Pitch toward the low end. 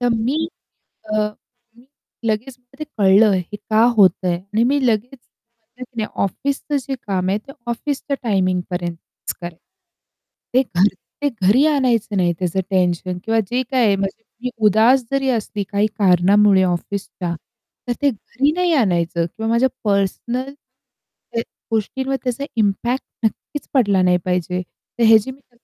No: high, 220 Hz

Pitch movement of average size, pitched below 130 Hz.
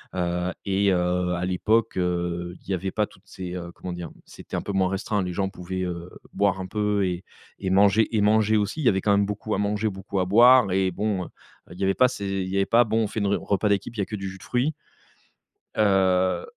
No: narrow, 2.2 semitones; very low, 95 Hz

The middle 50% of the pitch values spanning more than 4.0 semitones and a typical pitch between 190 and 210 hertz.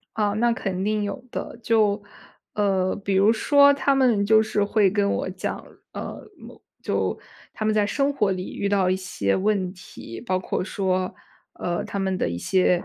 No: narrow, 2.6 semitones; high, 200 Hz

